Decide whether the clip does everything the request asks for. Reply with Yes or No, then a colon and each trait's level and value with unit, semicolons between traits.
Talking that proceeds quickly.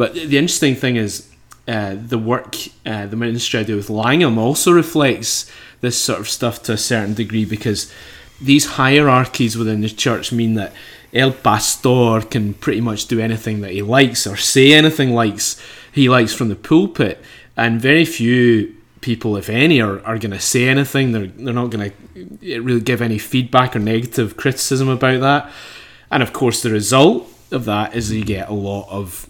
No: average, 190 wpm